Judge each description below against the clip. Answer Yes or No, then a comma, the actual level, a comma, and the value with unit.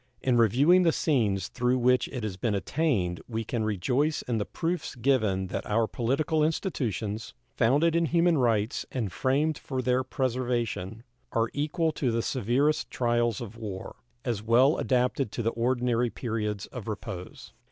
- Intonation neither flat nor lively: Yes, average, 3.8 semitones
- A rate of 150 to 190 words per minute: Yes, average, 160 wpm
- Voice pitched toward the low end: Yes, low, 120 Hz